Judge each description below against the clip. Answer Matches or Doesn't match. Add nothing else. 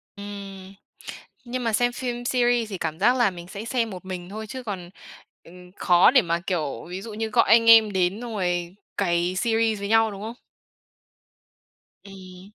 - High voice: Matches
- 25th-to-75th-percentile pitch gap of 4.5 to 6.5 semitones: Doesn't match